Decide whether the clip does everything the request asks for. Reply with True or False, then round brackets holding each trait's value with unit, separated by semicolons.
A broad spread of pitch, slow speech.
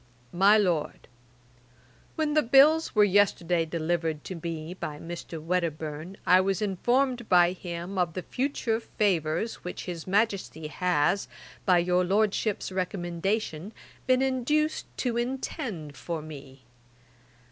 False (4.8 semitones; 125 wpm)